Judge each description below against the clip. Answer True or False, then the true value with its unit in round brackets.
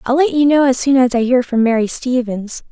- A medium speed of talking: False (265 wpm)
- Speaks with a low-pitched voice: False (250 Hz)